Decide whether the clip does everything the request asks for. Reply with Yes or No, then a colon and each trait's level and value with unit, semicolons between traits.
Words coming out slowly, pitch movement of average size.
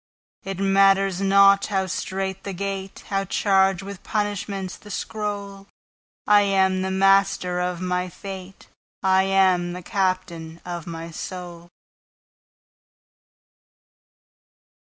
No: slow, 95 wpm; narrow, 1.5 semitones